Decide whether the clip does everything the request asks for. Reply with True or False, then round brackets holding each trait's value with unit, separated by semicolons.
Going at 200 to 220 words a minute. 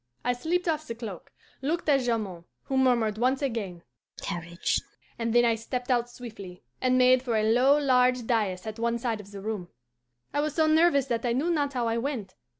True (205 wpm)